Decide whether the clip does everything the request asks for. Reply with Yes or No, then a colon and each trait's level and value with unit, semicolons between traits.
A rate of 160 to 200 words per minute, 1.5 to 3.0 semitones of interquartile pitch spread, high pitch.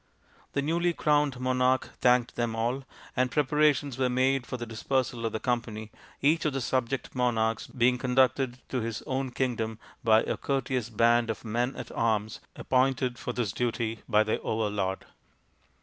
No: average, 165 wpm; narrow, 2.5 semitones; low, 125 Hz